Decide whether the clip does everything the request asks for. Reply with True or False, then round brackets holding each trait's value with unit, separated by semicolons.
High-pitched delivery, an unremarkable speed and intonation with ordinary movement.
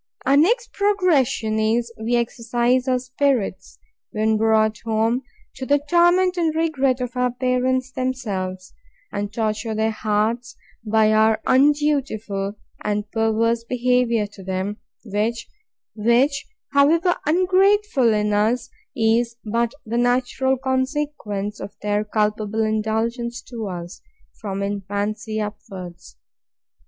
False (230 Hz; 115 wpm; 3.6 semitones)